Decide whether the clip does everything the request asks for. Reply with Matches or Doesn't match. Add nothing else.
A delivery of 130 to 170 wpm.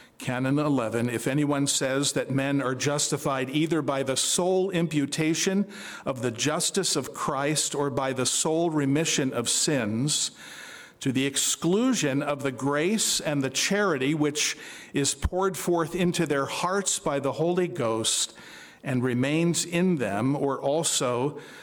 Matches